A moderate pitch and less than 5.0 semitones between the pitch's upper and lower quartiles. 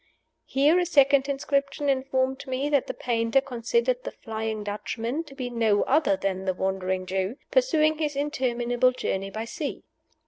No: very high, 255 Hz; average, 4.2 semitones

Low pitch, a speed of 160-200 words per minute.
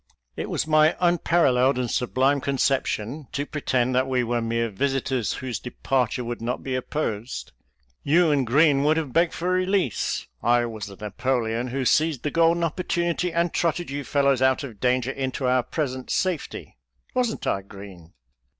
Yes: low, 130 Hz; average, 175 wpm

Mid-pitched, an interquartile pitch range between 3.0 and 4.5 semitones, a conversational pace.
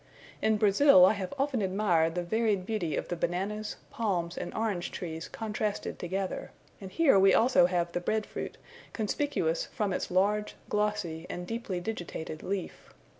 No: high, 195 Hz; average, 3.5 semitones; average, 160 wpm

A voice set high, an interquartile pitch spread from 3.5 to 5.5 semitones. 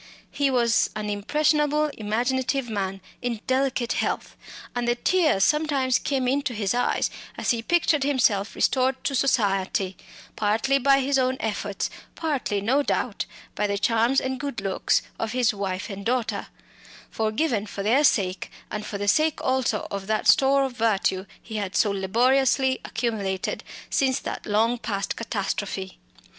Yes: high, 235 Hz; average, 4.6 semitones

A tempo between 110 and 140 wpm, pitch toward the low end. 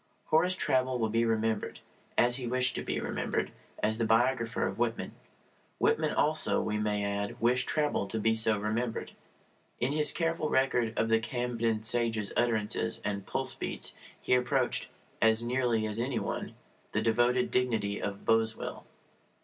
No: average, 155 wpm; low, 115 Hz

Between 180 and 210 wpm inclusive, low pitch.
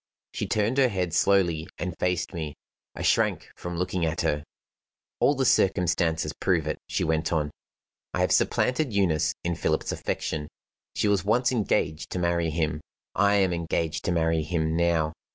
No: average, 170 wpm; very low, 85 Hz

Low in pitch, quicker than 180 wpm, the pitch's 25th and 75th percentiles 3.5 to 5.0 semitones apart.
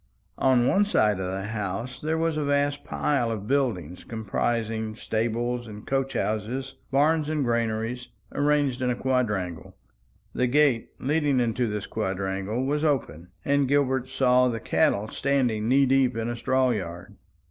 No: low, 125 Hz; average, 155 wpm; average, 4.0 semitones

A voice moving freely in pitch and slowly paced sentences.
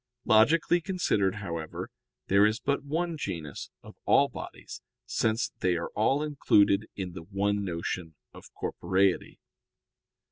Yes: wide, 7.2 semitones; slow, 130 wpm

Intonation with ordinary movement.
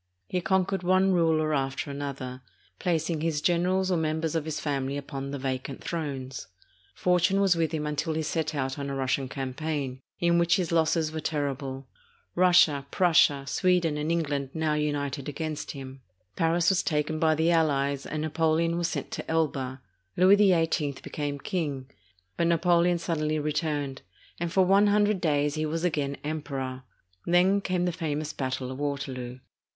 Yes: average, 3.4 semitones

